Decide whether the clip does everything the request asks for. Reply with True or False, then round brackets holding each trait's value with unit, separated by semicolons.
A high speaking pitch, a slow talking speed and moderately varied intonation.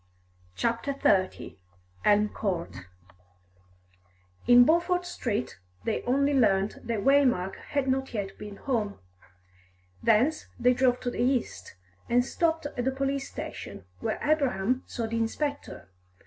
True (245 Hz; 125 wpm; 4.8 semitones)